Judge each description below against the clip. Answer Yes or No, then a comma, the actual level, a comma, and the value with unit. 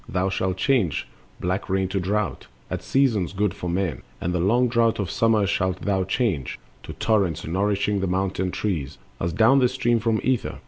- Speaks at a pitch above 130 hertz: No, very low, 95 Hz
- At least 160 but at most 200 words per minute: Yes, average, 185 wpm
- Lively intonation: No, average, 3.5 semitones